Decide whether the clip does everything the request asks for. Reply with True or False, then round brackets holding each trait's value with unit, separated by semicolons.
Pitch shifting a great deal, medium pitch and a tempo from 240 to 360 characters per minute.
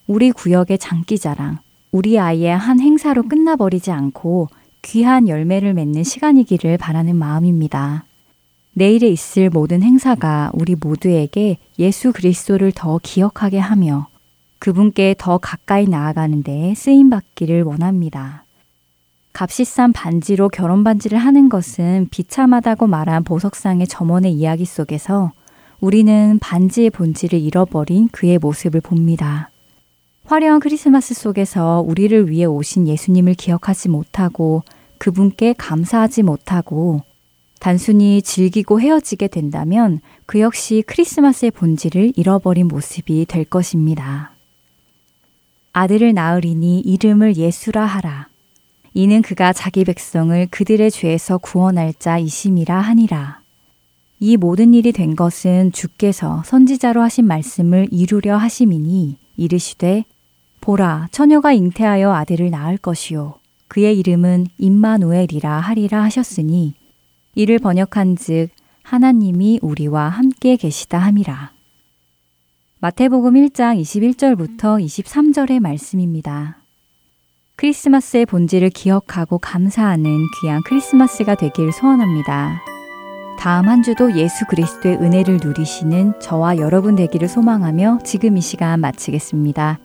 False (4.8 semitones; 180 Hz; 295 characters per minute)